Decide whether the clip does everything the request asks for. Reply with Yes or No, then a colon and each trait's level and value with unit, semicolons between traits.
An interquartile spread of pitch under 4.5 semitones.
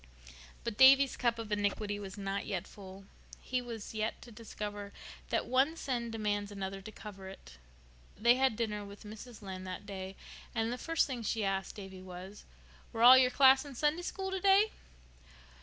Yes: average, 4.1 semitones